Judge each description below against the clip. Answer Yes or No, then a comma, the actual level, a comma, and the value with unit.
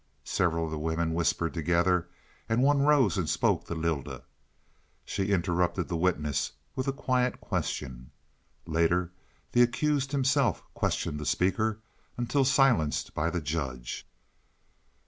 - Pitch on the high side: No, very low, 90 Hz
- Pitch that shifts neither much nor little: No, wide, 7.1 semitones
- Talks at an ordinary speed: No, slow, 130 wpm